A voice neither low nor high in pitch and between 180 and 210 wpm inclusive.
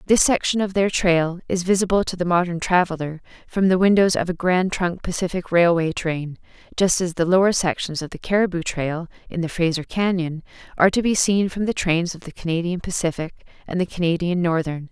Yes: medium, 175 Hz; average, 195 wpm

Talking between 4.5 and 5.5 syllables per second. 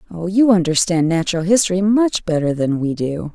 Yes: 5.4 syllables/s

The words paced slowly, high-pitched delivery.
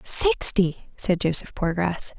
No: slow, 110 wpm; medium, 180 Hz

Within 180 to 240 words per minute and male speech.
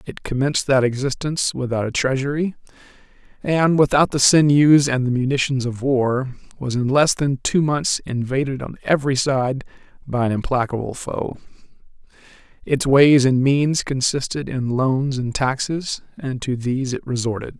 No: average, 150 wpm; male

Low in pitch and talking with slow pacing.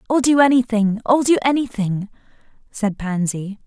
No: high, 225 Hz; slow, 115 wpm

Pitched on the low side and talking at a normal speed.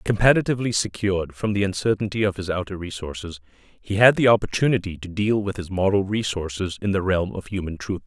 Yes: low, 100 Hz; average, 185 wpm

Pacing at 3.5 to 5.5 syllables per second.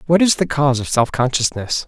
No: 5.9 syllables/s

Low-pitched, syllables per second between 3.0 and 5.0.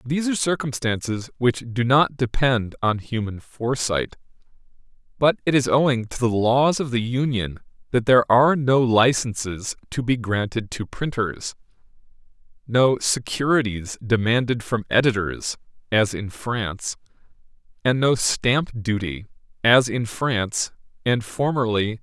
Yes: low, 120 Hz; 4.6 syllables/s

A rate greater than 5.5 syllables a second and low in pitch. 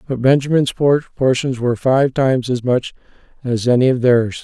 No: 4.9 syllables/s; low, 130 Hz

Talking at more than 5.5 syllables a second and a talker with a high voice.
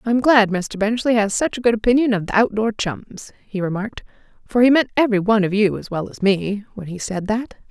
Yes: 5.7 syllables/s; high, 215 Hz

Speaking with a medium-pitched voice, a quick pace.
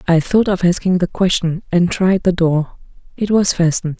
No: medium, 180 Hz; average, 195 wpm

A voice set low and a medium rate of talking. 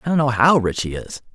No: low, 125 Hz; fast, 315 wpm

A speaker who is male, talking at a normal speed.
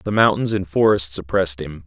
Yes: male; average, 195 wpm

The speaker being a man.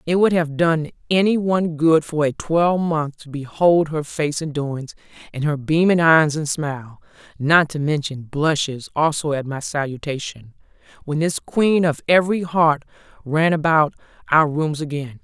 No: female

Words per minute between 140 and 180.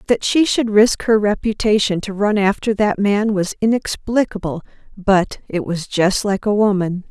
Yes: average, 170 wpm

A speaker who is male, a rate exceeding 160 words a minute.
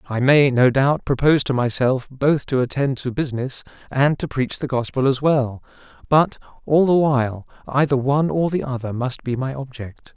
Yes: male; average, 190 wpm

